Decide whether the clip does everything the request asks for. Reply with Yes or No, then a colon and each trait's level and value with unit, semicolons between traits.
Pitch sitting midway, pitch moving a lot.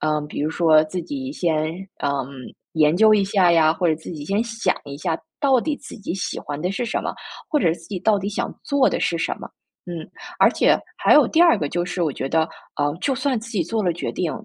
Yes: medium, 175 Hz; wide, 5.8 semitones